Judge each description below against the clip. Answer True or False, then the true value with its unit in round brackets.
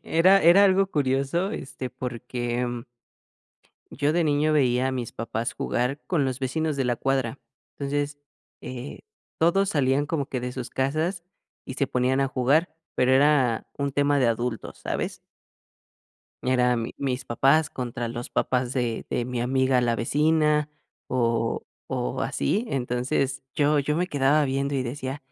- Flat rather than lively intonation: False (3.1 semitones)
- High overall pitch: False (135 Hz)